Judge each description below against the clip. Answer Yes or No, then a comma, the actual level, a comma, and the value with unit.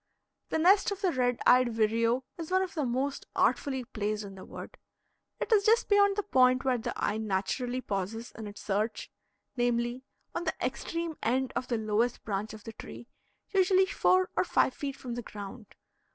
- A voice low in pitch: No, very high, 250 Hz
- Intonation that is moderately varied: No, wide, 6.4 semitones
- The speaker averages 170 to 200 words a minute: Yes, average, 190 wpm